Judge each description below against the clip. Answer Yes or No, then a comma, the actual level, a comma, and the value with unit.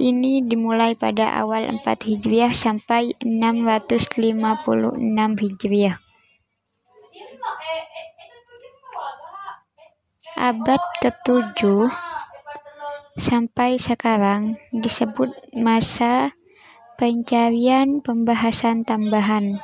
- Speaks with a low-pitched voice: No, high, 235 Hz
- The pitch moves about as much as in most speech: Yes, average, 4.5 semitones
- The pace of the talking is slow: Yes, slow, 55 wpm